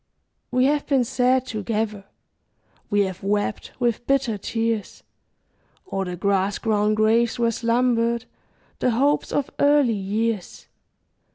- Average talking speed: No, slow, 120 wpm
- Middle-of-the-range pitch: No, high, 230 Hz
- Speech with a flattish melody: No, average, 3.2 semitones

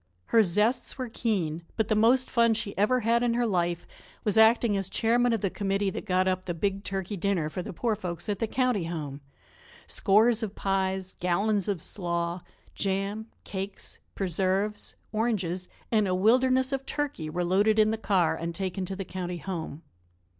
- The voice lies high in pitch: Yes, high, 195 Hz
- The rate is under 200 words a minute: Yes, average, 180 wpm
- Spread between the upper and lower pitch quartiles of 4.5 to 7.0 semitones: No, average, 3.6 semitones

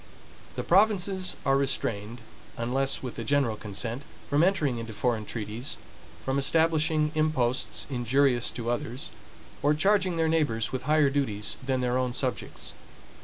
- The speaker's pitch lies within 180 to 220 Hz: No, low, 135 Hz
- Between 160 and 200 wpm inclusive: No, average, 140 wpm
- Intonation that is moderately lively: Yes, average, 4.5 semitones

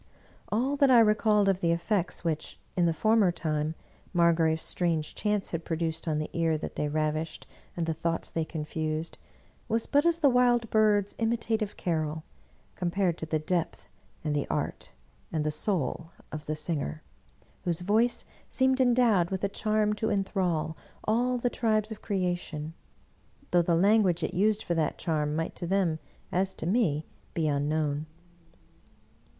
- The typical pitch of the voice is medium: Yes, medium, 175 Hz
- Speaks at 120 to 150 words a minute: No, average, 160 wpm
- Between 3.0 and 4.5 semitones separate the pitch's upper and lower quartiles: No, average, 5.2 semitones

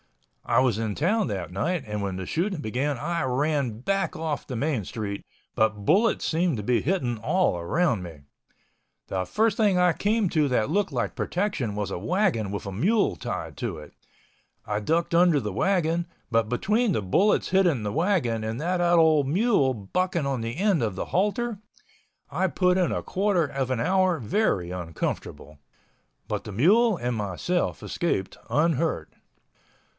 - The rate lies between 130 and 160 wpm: No, average, 170 wpm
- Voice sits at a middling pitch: Yes, medium, 145 Hz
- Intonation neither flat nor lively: No, wide, 9.0 semitones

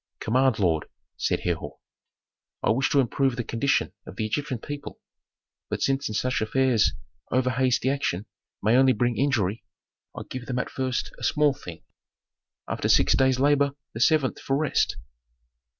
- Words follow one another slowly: No, average, 160 wpm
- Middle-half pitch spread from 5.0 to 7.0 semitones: No, average, 3.2 semitones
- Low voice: Yes, low, 130 Hz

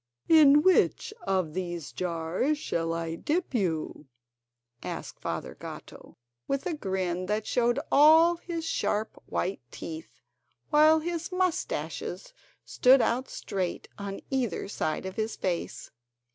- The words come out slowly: Yes, slow, 125 wpm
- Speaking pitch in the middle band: No, high, 220 Hz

